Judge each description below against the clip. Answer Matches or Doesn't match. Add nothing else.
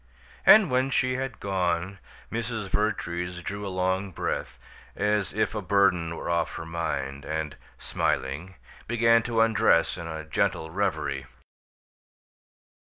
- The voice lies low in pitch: Matches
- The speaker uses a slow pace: Matches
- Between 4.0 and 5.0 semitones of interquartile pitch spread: Matches